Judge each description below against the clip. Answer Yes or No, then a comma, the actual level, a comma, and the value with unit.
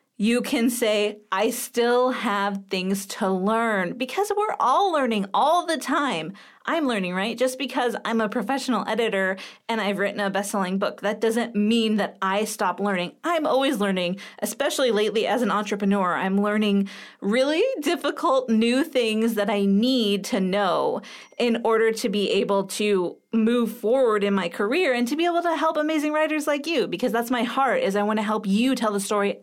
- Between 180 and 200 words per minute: Yes, average, 185 wpm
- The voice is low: No, high, 225 Hz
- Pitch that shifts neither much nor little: Yes, average, 4.3 semitones